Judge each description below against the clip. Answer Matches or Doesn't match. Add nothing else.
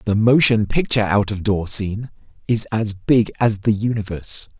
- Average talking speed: Matches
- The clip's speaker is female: Doesn't match